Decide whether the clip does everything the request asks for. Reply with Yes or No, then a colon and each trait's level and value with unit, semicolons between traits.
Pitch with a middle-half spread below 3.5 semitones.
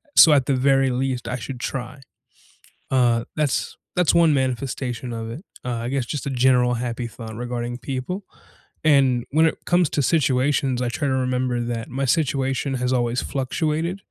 Yes: narrow, 2.4 semitones